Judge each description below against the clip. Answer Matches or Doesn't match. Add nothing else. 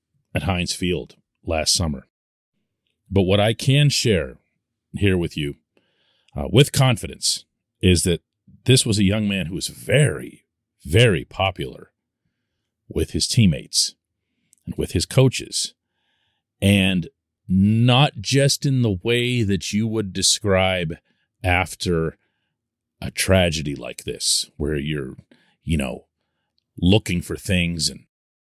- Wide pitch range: Doesn't match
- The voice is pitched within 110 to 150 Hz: Doesn't match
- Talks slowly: Matches